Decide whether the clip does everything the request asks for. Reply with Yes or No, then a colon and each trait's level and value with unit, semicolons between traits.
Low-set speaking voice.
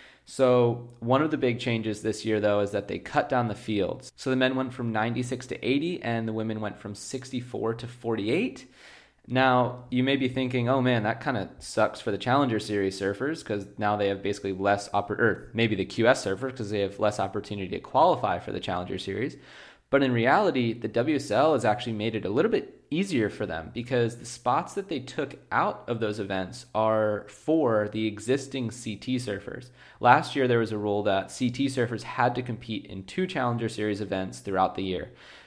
Yes: low, 115 Hz